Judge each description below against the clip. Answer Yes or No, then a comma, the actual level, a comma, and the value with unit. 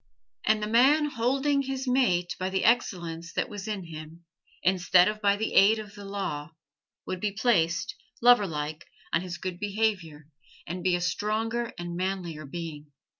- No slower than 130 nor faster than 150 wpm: No, average, 165 wpm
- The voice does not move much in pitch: No, average, 4.5 semitones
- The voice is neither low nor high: No, high, 195 Hz